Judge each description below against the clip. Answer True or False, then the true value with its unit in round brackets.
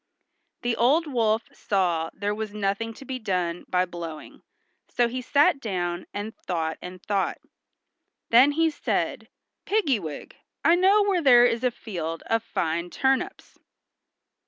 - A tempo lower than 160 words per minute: True (145 wpm)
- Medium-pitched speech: False (220 Hz)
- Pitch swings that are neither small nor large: False (6.8 semitones)